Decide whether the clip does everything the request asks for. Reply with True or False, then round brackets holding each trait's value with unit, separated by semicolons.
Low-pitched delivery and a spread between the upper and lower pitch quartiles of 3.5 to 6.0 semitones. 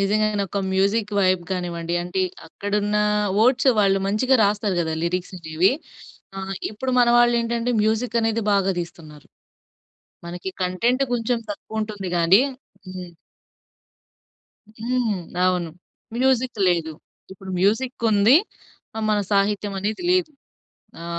False (205 Hz; 3.9 semitones)